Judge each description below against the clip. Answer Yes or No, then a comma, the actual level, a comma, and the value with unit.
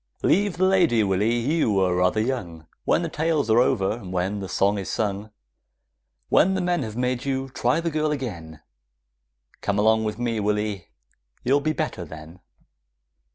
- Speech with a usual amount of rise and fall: No, wide, 6.6 semitones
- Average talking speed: Yes, average, 165 wpm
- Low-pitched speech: Yes, low, 110 Hz